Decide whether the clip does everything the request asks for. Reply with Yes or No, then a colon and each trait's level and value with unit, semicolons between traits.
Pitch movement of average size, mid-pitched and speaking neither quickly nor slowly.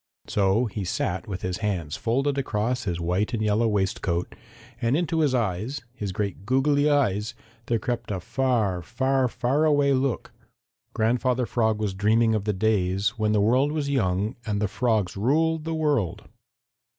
No: average, 4.8 semitones; low, 110 Hz; average, 165 wpm